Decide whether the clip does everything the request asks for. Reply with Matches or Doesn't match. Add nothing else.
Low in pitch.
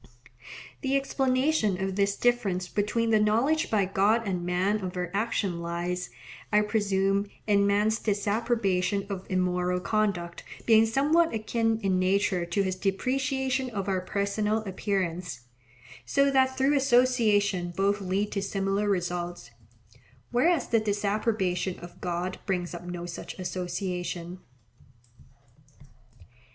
Doesn't match